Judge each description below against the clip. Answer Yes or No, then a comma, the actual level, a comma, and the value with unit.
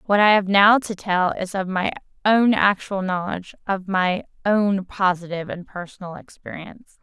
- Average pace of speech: Yes, average, 155 wpm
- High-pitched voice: Yes, high, 195 Hz